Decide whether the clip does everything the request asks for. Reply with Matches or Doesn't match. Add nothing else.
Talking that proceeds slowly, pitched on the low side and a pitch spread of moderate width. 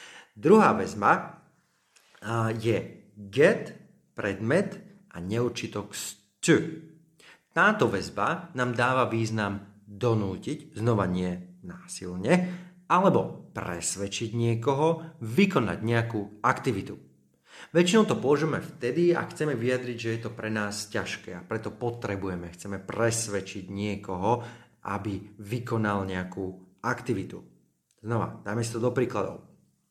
Doesn't match